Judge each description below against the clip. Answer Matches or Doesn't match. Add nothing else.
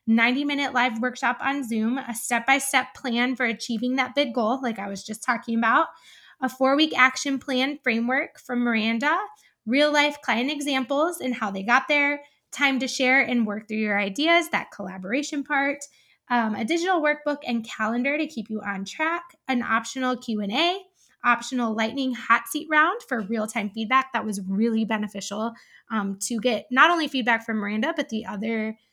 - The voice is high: Matches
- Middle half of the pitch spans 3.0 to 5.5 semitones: Matches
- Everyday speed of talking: Matches